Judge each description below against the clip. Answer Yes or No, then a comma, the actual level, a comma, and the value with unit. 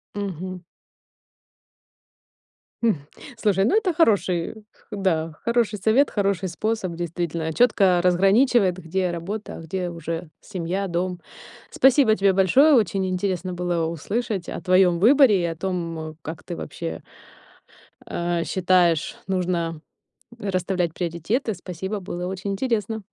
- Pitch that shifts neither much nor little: Yes, average, 3.2 semitones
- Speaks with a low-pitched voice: No, medium, 185 Hz